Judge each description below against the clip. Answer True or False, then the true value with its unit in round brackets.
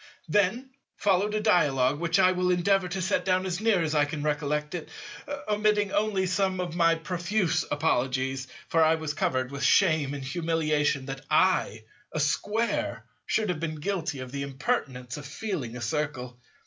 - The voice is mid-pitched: True (160 Hz)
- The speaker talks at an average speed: True (170 wpm)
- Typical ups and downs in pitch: True (4.8 semitones)